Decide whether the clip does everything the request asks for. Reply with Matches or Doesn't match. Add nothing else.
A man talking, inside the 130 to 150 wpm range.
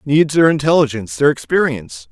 Matches